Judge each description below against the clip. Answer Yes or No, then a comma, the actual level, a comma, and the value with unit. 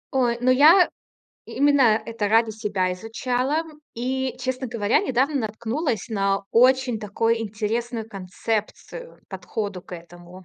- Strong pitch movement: No, average, 3.8 semitones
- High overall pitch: Yes, high, 230 Hz